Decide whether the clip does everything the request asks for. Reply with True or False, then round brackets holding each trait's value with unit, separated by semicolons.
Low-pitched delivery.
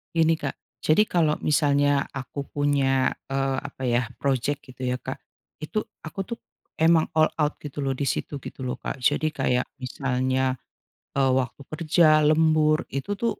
False (145 Hz)